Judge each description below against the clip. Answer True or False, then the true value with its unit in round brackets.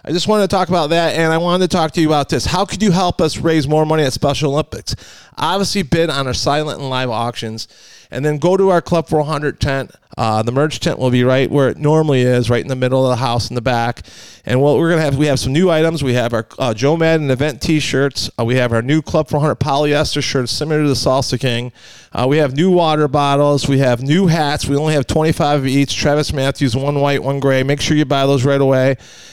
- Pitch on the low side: False (145 Hz)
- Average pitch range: True (3.3 semitones)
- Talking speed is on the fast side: True (260 wpm)